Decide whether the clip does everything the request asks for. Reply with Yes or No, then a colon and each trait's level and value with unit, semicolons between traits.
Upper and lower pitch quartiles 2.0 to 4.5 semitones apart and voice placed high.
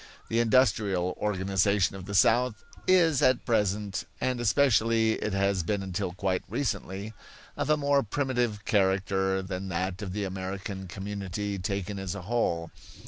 No: average, 3.0 semitones; low, 100 Hz